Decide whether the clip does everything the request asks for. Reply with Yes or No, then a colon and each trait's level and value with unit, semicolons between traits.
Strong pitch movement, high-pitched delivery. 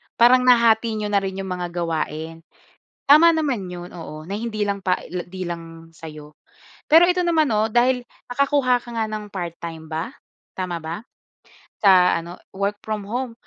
Yes: wide, 5.8 semitones; high, 200 Hz